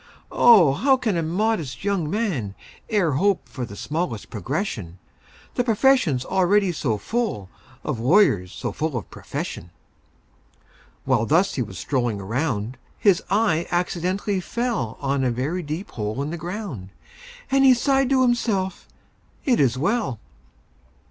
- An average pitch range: No, wide, 8.8 semitones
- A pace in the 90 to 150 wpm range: Yes, average, 140 wpm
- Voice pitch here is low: No, medium, 165 Hz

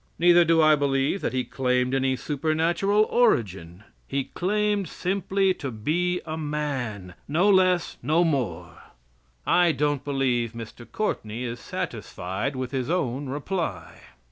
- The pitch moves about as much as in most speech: No, wide, 5.7 semitones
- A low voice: No, medium, 145 Hz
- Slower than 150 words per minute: Yes, slow, 135 wpm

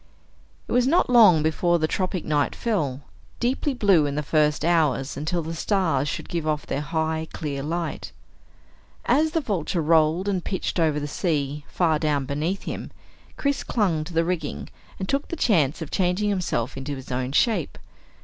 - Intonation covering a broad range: No, average, 4.2 semitones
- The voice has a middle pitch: Yes, medium, 160 Hz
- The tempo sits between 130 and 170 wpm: No, average, 180 wpm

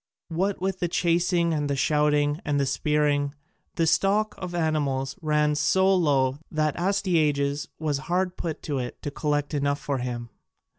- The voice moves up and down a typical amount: Yes, average, 3.4 semitones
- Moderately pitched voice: Yes, medium, 150 Hz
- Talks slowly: No, average, 160 wpm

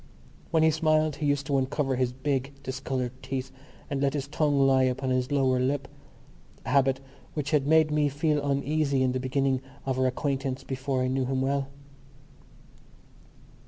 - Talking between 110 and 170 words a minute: Yes, average, 165 wpm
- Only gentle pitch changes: Yes, narrow, 1.7 semitones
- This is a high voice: No, low, 135 Hz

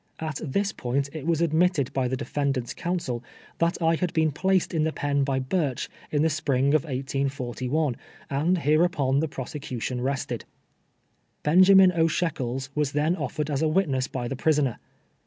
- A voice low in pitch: No, medium, 145 Hz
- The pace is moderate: Yes, average, 165 wpm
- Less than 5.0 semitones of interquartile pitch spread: Yes, average, 3.5 semitones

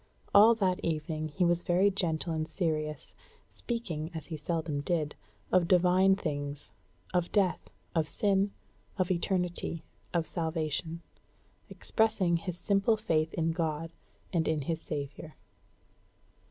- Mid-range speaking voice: Yes, medium, 170 Hz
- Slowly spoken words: Yes, slow, 125 wpm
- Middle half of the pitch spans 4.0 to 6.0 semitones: No, average, 2.9 semitones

